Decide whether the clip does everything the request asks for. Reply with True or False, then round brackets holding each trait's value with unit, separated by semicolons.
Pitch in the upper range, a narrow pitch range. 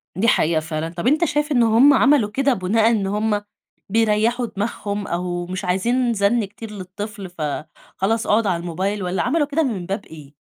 False (205 Hz; 4.3 semitones)